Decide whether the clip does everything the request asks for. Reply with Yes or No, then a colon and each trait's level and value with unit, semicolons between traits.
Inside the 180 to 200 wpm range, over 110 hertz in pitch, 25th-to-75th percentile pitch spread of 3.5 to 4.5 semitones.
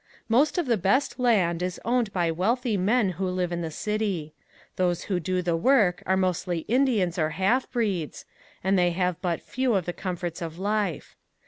Yes: average, 190 wpm; medium, 185 Hz; average, 4.0 semitones